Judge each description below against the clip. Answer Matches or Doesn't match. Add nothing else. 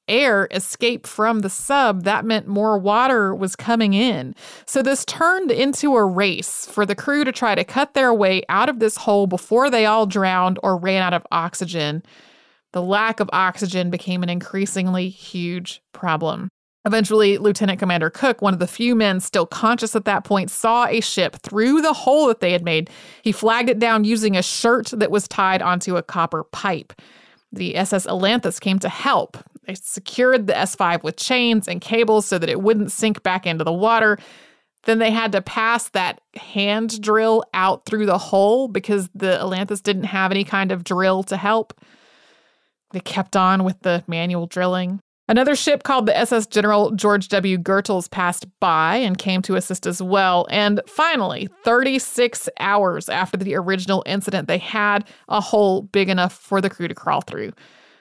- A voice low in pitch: Doesn't match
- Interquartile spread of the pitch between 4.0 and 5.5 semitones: Doesn't match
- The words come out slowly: Doesn't match